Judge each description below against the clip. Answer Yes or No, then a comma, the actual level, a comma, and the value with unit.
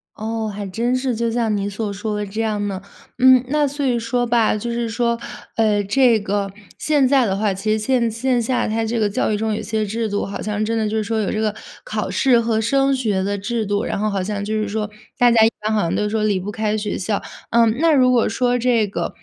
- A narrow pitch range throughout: Yes, narrow, 2.3 semitones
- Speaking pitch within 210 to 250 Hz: Yes, high, 220 Hz